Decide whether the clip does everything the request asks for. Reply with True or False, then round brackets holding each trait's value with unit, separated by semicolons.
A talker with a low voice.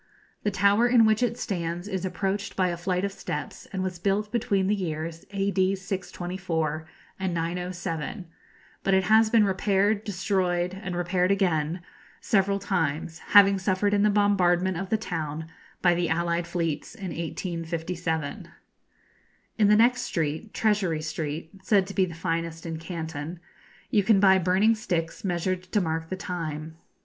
False (185 Hz)